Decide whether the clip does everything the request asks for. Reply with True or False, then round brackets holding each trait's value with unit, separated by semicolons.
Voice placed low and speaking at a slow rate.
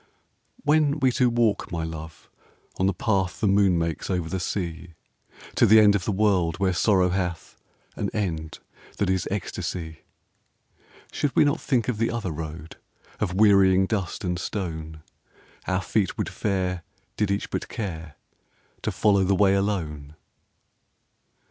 False (95 Hz; 155 wpm)